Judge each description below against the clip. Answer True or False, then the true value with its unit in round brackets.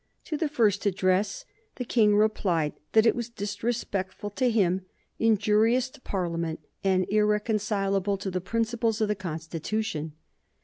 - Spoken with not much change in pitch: False (3.2 semitones)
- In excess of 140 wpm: False (135 wpm)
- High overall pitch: True (210 Hz)